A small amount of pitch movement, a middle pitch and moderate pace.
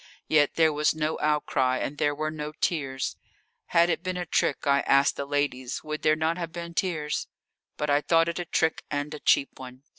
No: narrow, 2.3 semitones; medium, 150 Hz; fast, 210 wpm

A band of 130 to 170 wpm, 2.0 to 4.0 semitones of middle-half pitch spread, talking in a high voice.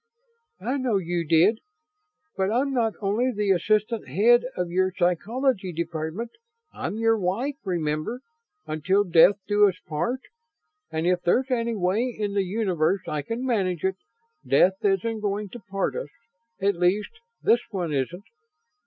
No: average, 150 wpm; average, 4.4 semitones; high, 200 Hz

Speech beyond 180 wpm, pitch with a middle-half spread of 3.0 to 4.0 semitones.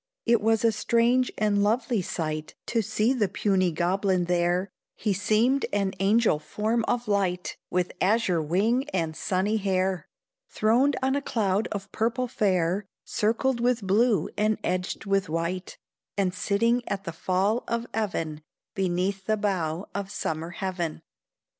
No: average, 145 wpm; average, 3.7 semitones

